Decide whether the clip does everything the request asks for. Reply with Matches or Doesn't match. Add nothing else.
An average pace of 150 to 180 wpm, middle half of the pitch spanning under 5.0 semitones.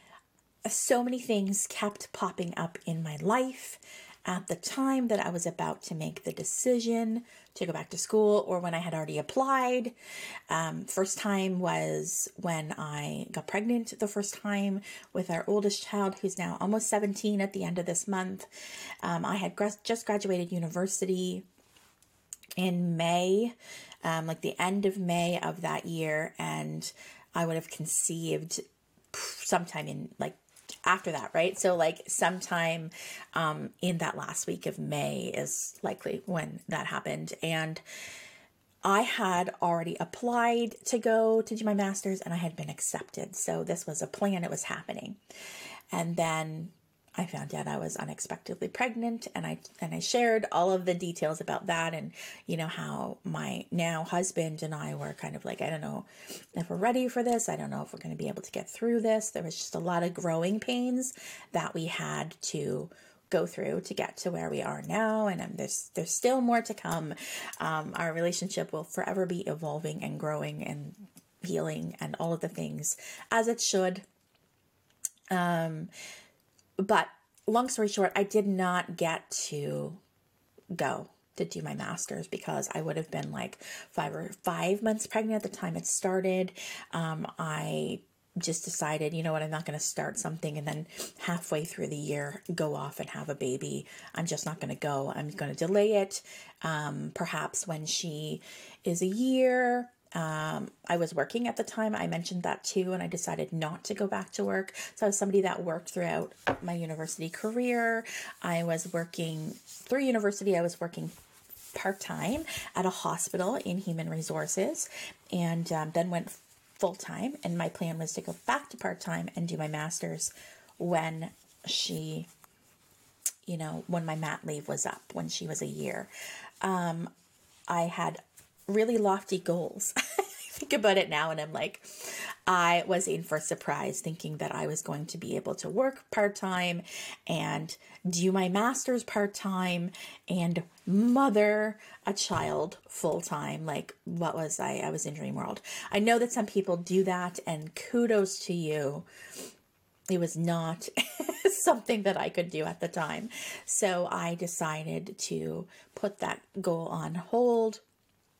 Matches